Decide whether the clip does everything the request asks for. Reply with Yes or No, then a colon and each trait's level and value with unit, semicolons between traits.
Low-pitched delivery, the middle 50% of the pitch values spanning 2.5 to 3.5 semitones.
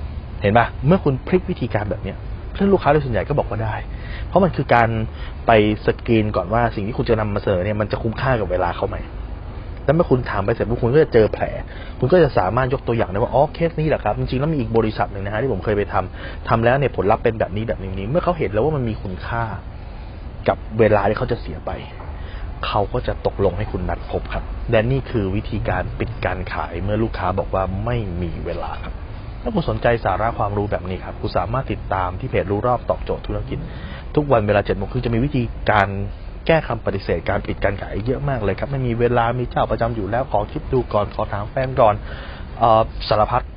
No: low, 105 Hz; average, 4.3 semitones